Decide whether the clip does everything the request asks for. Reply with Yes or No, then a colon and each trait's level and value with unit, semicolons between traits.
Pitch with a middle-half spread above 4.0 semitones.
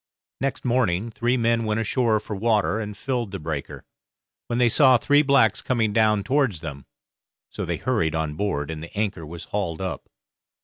Yes: wide, 5.6 semitones